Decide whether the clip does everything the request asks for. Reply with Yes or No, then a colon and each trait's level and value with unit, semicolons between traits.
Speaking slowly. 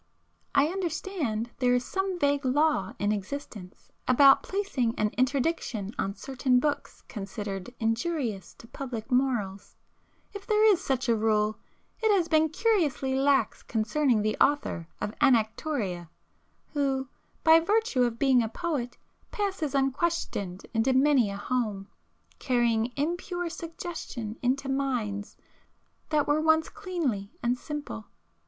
Yes: slow, 125 wpm